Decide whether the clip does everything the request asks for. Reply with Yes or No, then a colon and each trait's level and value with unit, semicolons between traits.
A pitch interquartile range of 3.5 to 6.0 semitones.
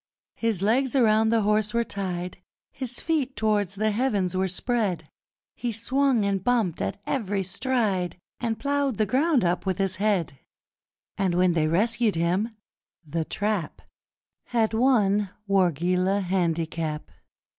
Yes: average, 4.3 semitones